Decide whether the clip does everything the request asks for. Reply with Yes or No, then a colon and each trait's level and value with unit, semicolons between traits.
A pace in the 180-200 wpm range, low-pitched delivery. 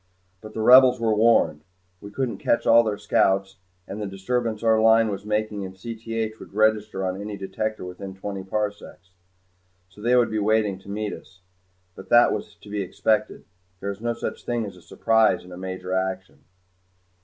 Yes: average, 185 wpm; low, 105 Hz